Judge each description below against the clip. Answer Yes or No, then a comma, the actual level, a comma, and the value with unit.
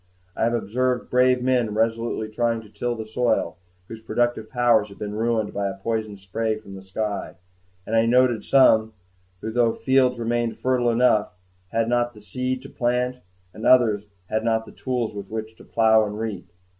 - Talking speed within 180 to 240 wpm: Yes, average, 190 wpm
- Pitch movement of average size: No, narrow, 2.1 semitones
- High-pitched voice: No, low, 115 Hz